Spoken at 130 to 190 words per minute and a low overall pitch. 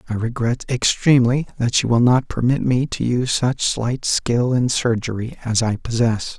Yes: average, 180 wpm; low, 120 Hz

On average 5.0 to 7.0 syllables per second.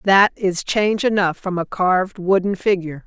Yes: 5.1 syllables/s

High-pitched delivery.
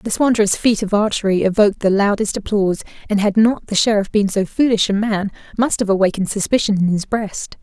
Yes: high, 205 Hz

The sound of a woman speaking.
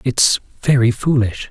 No: male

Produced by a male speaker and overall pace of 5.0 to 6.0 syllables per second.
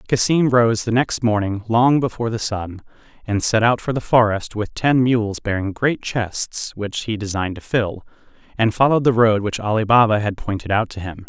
Yes: male; 5.1 syllables/s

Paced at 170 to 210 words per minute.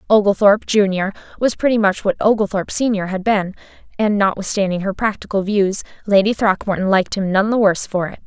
Yes: average, 175 wpm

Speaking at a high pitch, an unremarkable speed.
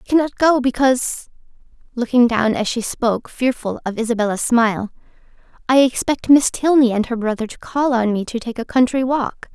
Yes: high, 245 Hz; average, 170 wpm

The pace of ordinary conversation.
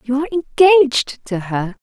Yes: average, 165 wpm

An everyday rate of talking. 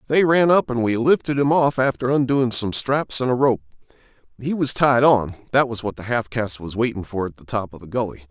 No: fast, 245 wpm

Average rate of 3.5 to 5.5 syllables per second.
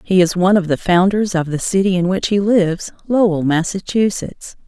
Yes: 5.3 syllables/s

